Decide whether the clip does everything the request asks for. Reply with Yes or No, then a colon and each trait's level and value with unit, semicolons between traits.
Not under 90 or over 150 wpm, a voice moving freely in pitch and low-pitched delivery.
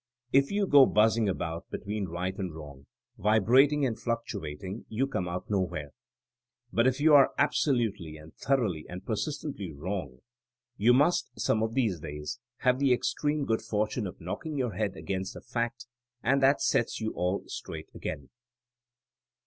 No: average, 165 wpm; wide, 6.4 semitones; low, 110 Hz